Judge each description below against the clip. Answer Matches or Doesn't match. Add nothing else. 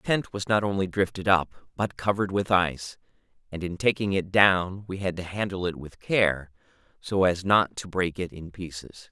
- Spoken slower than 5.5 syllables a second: Matches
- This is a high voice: Doesn't match